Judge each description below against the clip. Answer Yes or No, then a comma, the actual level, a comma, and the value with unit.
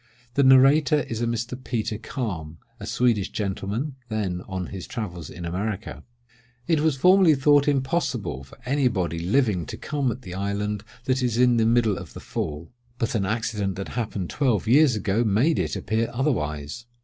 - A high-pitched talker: No, low, 115 Hz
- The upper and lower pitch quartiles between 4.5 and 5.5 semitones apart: Yes, average, 5.2 semitones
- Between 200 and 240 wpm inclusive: No, average, 175 wpm